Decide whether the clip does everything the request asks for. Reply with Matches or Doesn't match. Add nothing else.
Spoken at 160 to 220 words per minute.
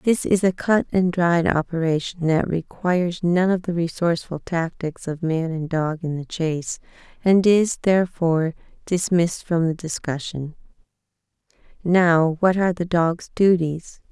Doesn't match